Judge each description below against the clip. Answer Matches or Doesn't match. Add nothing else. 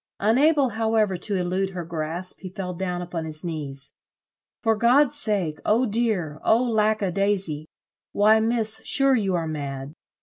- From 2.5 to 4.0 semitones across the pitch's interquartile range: Doesn't match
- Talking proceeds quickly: Doesn't match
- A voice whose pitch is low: Doesn't match